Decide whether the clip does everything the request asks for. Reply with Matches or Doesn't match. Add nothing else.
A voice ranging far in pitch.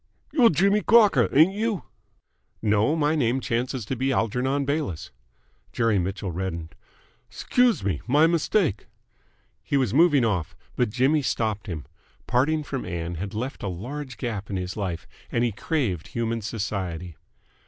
Matches